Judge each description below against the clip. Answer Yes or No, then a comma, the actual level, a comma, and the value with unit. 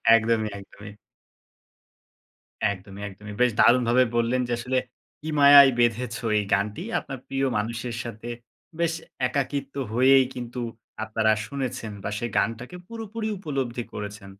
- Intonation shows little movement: No, average, 3.7 semitones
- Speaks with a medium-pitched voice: No, low, 120 Hz